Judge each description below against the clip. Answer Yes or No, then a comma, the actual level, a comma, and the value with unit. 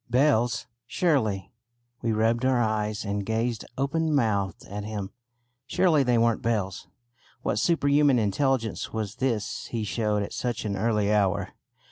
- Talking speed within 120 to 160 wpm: Yes, average, 140 wpm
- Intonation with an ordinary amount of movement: Yes, average, 3.6 semitones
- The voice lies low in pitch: Yes, low, 115 Hz